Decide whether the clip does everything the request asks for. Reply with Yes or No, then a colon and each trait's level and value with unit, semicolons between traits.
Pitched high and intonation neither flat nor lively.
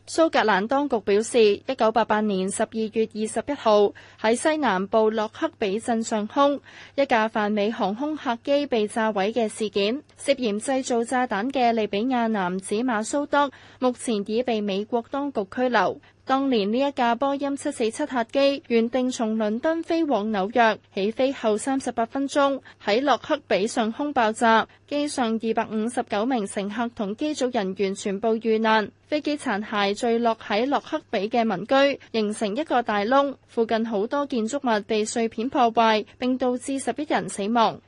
Yes: high, 230 Hz; average, 3.7 semitones